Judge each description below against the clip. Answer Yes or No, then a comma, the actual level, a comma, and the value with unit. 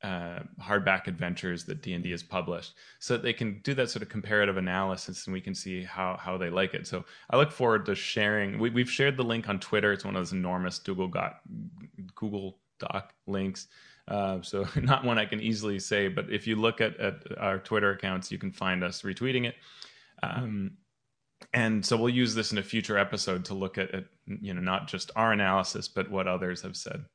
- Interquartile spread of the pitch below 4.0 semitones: Yes, average, 3.0 semitones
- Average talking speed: No, fast, 220 wpm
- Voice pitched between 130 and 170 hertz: No, low, 100 Hz